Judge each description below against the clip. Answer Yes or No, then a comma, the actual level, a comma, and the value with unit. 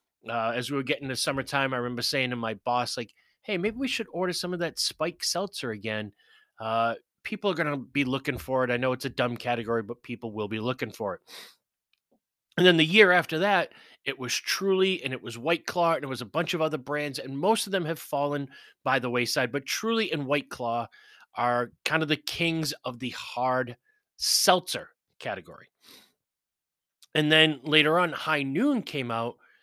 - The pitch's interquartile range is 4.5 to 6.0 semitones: Yes, average, 5.3 semitones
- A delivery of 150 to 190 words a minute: No, fast, 205 wpm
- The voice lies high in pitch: No, medium, 140 Hz